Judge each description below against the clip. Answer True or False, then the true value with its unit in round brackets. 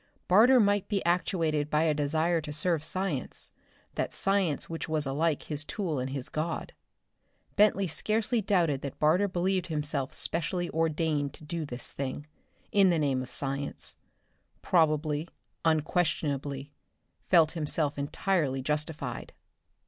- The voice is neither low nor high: True (155 Hz)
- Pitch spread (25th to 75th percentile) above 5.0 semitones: False (3.4 semitones)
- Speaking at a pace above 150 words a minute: False (135 wpm)